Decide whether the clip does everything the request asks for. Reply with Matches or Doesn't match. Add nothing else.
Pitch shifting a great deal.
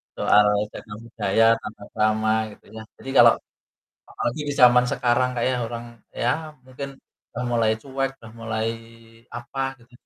Doesn't match